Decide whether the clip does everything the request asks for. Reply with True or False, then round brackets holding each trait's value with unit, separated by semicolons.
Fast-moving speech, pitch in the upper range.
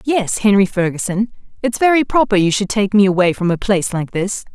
True (210 wpm; 205 Hz)